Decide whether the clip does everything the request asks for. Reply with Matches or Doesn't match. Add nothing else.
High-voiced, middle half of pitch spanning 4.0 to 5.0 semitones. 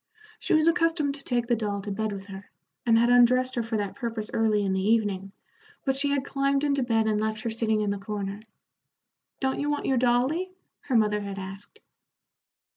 Matches